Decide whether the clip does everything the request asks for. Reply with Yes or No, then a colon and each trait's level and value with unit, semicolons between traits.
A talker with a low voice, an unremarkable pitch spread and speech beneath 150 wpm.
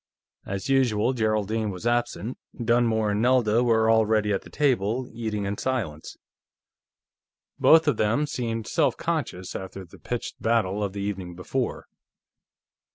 Yes: low, 110 Hz; average, 3.0 semitones; average, 140 wpm